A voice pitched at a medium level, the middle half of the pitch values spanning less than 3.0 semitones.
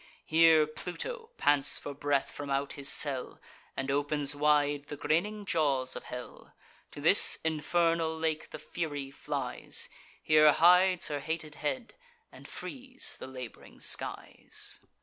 Yes: medium, 150 Hz; narrow, 2.6 semitones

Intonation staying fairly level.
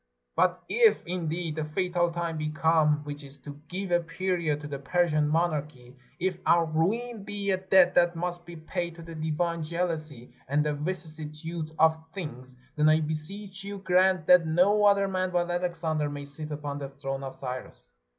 No: average, 3.0 semitones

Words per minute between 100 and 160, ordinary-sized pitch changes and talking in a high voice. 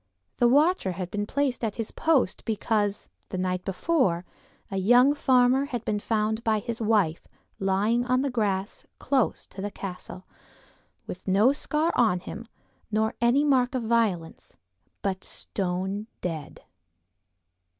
Yes: average, 140 wpm; average, 4.5 semitones; high, 220 Hz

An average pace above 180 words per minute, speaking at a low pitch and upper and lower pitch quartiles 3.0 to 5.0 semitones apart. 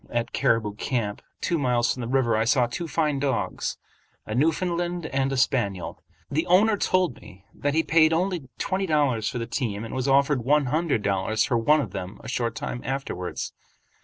No: average, 190 wpm; low, 130 Hz; wide, 5.4 semitones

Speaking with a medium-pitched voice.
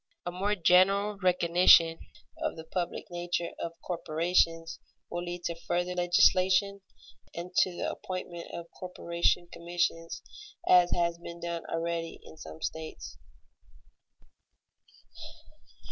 Yes: medium, 175 Hz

